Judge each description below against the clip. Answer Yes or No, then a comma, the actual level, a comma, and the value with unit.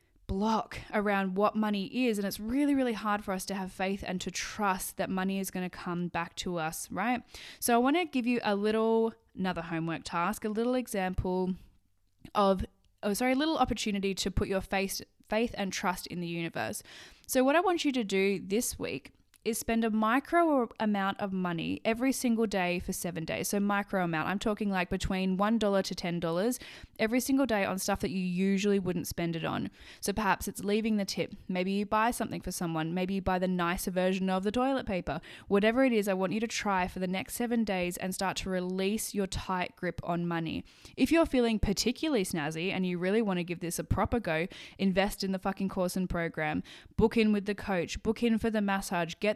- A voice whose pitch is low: No, high, 195 Hz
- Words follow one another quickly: Yes, fast, 220 wpm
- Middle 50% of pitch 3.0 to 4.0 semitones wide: Yes, average, 3.4 semitones